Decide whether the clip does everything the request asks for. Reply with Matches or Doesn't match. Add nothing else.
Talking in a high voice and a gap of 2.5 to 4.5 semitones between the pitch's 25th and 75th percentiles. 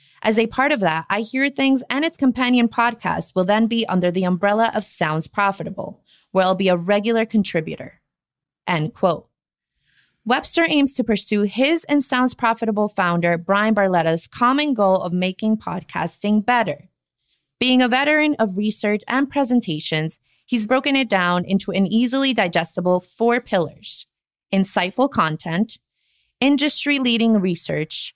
Doesn't match